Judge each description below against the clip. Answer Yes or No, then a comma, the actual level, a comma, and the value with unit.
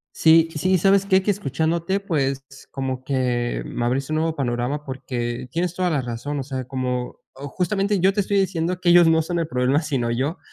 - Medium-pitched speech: Yes, medium, 150 Hz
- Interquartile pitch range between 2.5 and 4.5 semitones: No, average, 5.3 semitones